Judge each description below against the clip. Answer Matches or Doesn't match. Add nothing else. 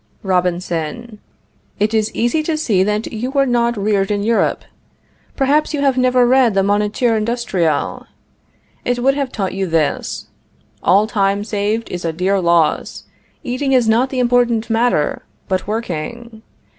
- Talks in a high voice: Matches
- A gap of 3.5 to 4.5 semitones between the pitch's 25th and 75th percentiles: Matches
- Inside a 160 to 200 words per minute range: Doesn't match